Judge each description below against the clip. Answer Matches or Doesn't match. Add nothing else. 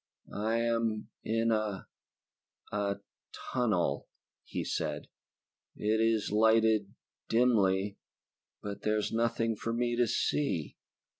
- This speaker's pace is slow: Matches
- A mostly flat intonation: Matches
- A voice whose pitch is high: Doesn't match